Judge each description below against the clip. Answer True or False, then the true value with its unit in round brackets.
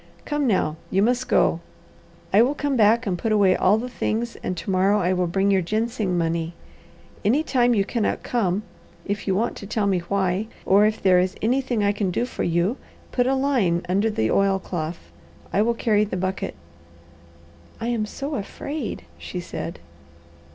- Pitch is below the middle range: False (205 Hz)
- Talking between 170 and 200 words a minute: True (180 wpm)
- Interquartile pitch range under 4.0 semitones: False (4.3 semitones)